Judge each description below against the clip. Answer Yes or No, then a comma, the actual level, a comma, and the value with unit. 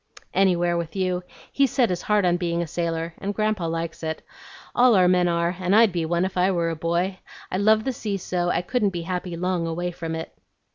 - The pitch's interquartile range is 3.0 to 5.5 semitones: No, narrow, 2.4 semitones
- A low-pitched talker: No, medium, 180 Hz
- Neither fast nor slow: No, fast, 230 wpm